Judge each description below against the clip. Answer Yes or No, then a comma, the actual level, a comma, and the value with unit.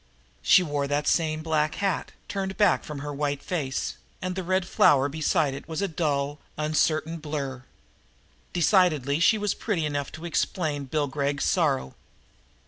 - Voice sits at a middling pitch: Yes, medium, 155 Hz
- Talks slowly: No, average, 155 wpm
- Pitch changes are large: No, average, 3.5 semitones